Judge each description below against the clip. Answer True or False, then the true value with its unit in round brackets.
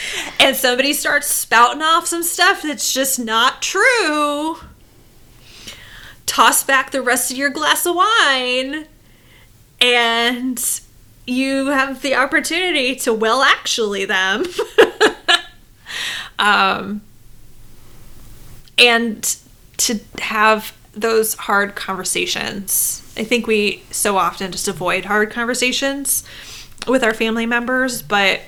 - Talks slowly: True (105 wpm)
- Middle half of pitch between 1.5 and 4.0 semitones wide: False (5.2 semitones)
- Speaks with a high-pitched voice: True (245 Hz)